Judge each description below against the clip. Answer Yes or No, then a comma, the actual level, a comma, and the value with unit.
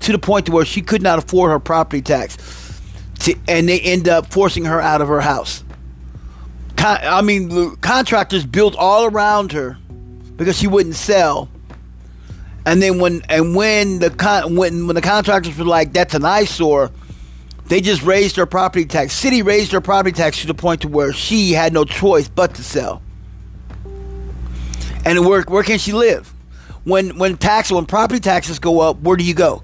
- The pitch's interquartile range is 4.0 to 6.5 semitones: Yes, average, 5.2 semitones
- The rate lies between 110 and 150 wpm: No, average, 190 wpm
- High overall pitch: No, medium, 170 Hz